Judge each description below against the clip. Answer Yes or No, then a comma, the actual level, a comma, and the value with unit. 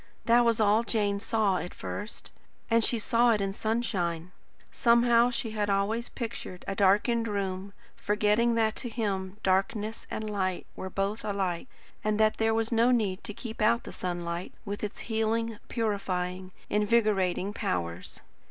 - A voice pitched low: No, high, 210 Hz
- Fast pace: No, average, 155 wpm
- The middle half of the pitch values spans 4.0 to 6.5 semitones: No, average, 2.9 semitones